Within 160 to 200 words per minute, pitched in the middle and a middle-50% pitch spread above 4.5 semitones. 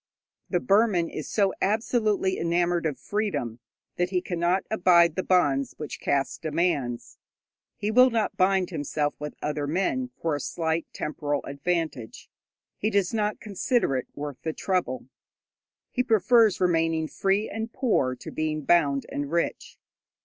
No: average, 145 wpm; medium, 175 Hz; average, 5.3 semitones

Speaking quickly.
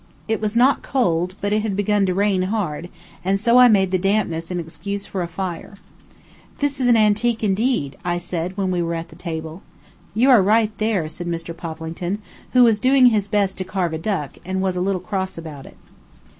Yes: fast, 210 wpm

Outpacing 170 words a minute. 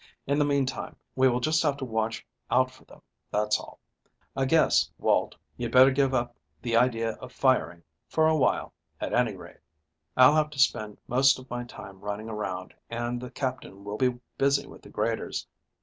Yes: average, 190 wpm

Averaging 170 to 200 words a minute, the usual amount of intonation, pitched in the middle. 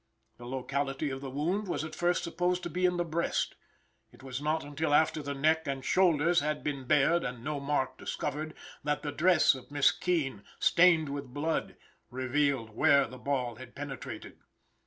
Yes: average, 180 wpm; average, 3.1 semitones; medium, 145 Hz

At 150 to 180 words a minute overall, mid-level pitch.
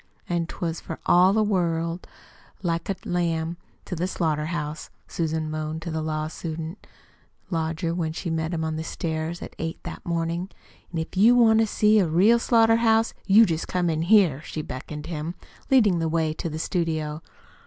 No: average, 190 wpm; medium, 165 Hz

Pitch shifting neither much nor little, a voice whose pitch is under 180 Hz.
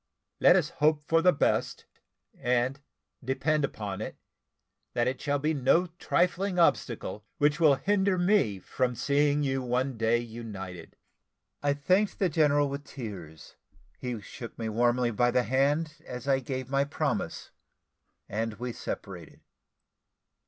Yes: average, 4.1 semitones; low, 135 Hz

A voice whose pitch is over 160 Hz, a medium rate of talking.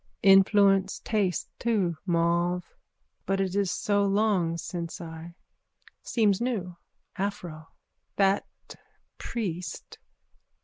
No: high, 190 Hz; slow, 95 wpm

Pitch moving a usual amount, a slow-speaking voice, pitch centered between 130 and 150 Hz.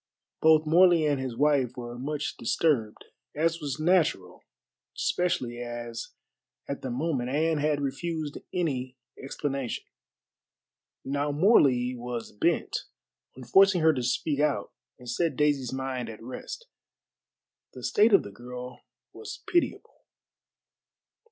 Yes: average, 4.3 semitones; slow, 125 wpm; medium, 140 Hz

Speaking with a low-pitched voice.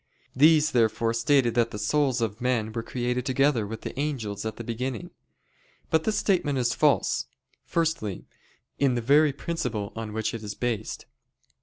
Yes: low, 120 Hz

